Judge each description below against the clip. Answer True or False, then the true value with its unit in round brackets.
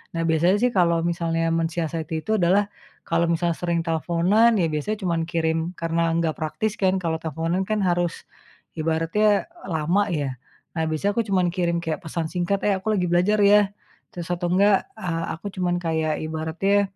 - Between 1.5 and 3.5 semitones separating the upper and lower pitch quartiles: True (2.8 semitones)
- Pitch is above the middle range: False (170 Hz)